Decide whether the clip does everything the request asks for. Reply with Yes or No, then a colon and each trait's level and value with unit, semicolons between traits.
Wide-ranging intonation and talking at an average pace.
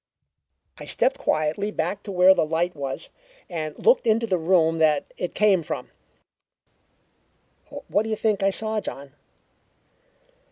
No: average, 4.9 semitones; average, 145 wpm